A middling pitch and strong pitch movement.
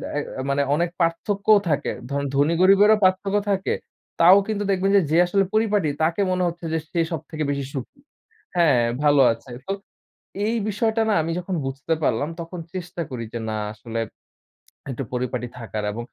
Yes: medium, 170 Hz; wide, 5.9 semitones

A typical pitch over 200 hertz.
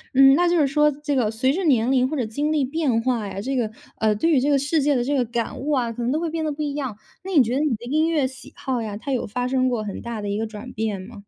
Yes: very high, 260 Hz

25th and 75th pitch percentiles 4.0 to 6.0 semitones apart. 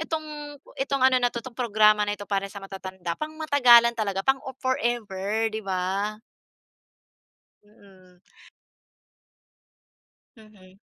Yes: average, 4.3 semitones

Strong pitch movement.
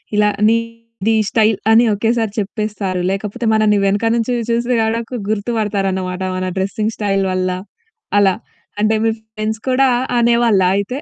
No: narrow, 2.6 semitones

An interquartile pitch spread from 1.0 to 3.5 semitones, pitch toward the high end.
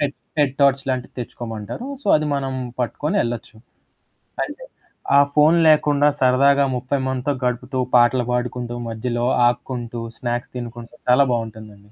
No: average, 2.7 semitones; low, 125 Hz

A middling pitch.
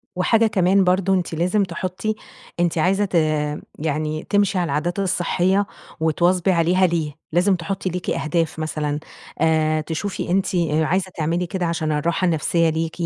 Yes: medium, 175 Hz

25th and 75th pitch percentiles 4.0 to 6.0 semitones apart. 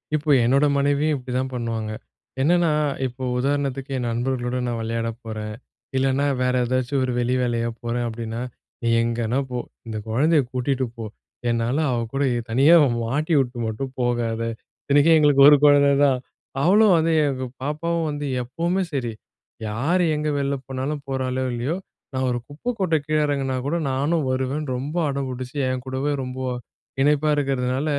No: average, 3.1 semitones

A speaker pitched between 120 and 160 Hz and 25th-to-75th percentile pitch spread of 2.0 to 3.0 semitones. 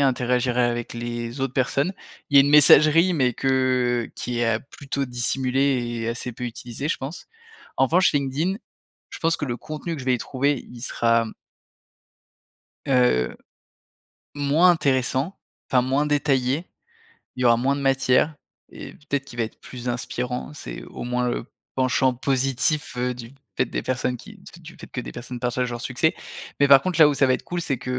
Yes: low, 130 Hz; narrow, 2.6 semitones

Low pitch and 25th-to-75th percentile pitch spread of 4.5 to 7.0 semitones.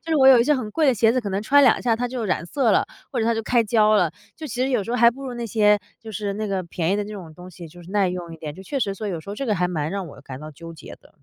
No: high, 210 Hz; average, 5.0 semitones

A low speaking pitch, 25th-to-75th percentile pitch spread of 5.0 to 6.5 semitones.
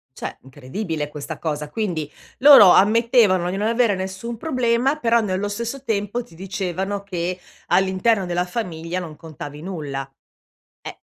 No: high, 190 Hz; wide, 5.4 semitones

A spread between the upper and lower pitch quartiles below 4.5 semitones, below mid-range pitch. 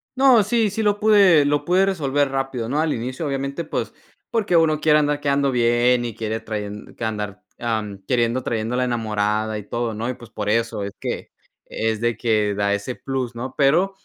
No: average, 5.1 semitones; low, 125 Hz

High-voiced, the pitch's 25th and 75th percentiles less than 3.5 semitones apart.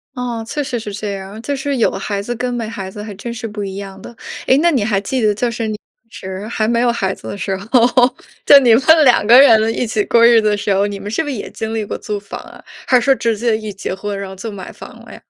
Yes: high, 220 Hz; average, 2.9 semitones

